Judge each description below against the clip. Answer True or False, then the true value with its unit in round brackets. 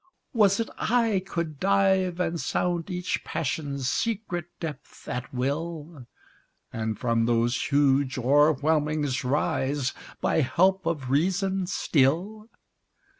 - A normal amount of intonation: False (5.8 semitones)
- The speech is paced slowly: True (105 wpm)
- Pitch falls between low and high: True (155 Hz)